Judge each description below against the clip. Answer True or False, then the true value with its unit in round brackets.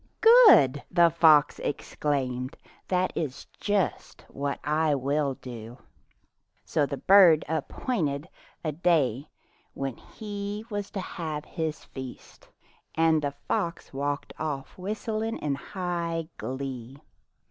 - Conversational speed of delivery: False (115 wpm)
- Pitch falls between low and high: True (155 Hz)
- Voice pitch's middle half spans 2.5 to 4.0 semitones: False (4.4 semitones)